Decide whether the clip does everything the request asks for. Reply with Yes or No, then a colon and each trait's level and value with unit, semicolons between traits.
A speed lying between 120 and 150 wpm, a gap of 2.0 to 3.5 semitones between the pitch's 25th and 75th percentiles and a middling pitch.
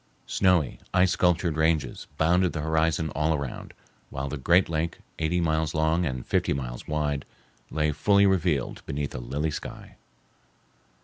No: average, 145 wpm; average, 2.8 semitones; very low, 80 Hz